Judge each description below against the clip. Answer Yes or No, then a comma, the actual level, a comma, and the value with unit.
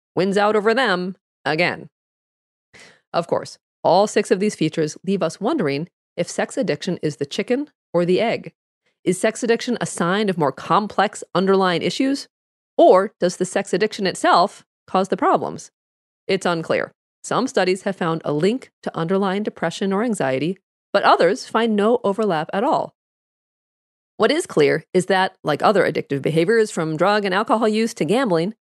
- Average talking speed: Yes, average, 165 wpm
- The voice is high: Yes, high, 195 Hz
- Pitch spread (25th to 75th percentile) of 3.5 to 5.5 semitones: Yes, average, 3.8 semitones